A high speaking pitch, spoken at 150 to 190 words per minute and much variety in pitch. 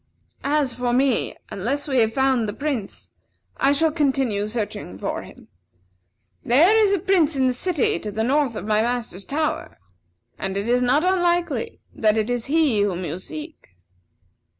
Yes: very high, 255 Hz; average, 170 wpm; wide, 5.9 semitones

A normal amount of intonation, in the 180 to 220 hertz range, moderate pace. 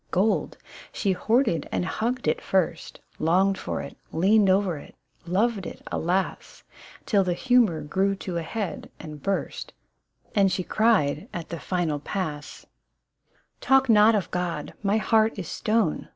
Yes: average, 4.2 semitones; high, 190 Hz; average, 160 wpm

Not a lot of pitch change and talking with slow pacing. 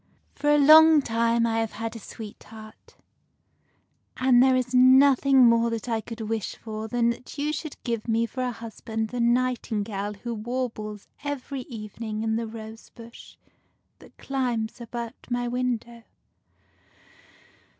No: narrow, 2.3 semitones; average, 150 wpm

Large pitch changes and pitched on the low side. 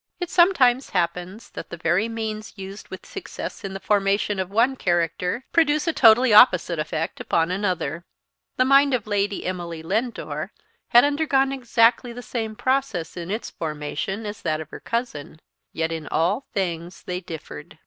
No: wide, 6.0 semitones; high, 205 Hz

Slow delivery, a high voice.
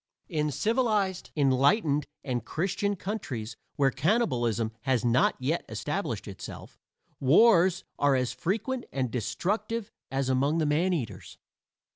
No: slow, 115 wpm; medium, 150 Hz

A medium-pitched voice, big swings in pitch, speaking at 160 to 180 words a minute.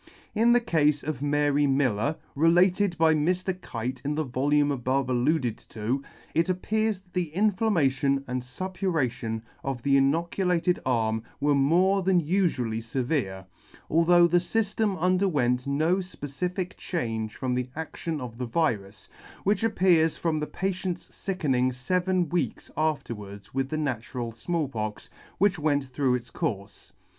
No: medium, 150 Hz; wide, 6.0 semitones; average, 145 wpm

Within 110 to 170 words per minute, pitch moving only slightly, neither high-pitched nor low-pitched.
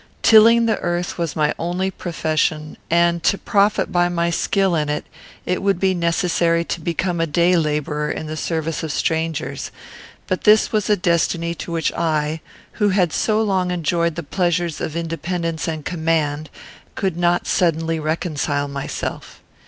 Yes: average, 160 wpm; narrow, 2.2 semitones; medium, 170 Hz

